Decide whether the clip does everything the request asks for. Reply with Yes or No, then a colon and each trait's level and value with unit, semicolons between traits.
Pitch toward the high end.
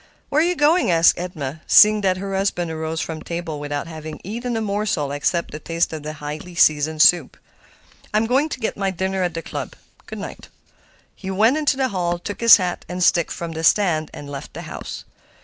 No: medium, 175 Hz